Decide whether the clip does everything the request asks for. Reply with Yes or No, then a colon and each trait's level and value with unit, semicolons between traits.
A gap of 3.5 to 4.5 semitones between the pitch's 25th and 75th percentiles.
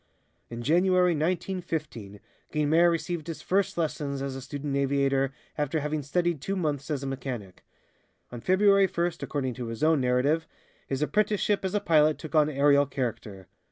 Yes: average, 4.2 semitones